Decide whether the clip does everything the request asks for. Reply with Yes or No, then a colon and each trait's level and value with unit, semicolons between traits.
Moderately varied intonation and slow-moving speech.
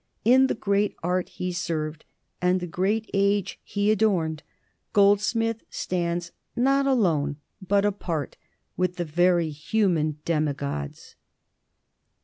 Yes: average, 4.0 semitones; slow, 115 wpm